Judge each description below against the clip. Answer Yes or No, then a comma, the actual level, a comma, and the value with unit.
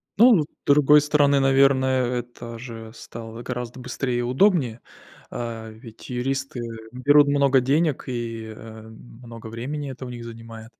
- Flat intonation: No, average, 3.1 semitones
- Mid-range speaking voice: No, low, 125 Hz